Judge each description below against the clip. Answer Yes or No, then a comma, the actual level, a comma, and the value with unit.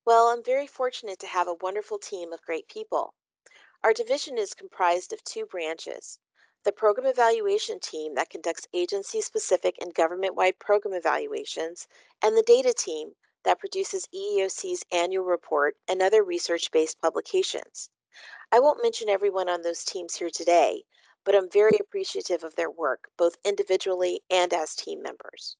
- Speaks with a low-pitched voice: No, high, 230 Hz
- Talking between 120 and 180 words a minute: Yes, average, 160 wpm